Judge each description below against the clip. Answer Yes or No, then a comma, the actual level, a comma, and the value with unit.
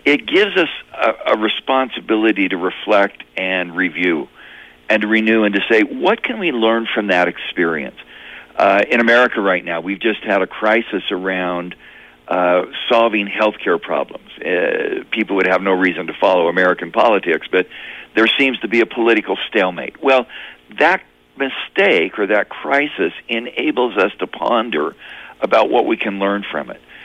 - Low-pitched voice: Yes, low, 110 Hz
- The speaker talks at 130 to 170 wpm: Yes, average, 165 wpm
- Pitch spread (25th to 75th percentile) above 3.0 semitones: Yes, average, 3.8 semitones